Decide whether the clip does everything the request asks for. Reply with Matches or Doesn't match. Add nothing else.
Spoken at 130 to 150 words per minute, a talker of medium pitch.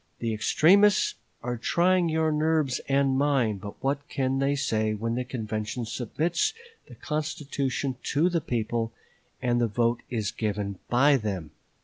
Doesn't match